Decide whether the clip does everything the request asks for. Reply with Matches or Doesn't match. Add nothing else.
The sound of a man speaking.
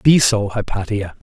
Matches